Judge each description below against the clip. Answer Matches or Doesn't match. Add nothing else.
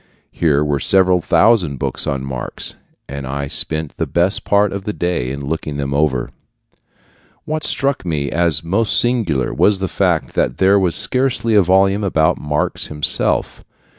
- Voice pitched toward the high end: Doesn't match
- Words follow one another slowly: Doesn't match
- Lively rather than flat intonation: Matches